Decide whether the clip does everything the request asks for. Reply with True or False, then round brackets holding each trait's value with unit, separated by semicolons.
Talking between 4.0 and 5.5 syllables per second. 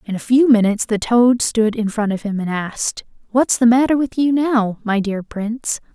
True (5.0 syllables/s)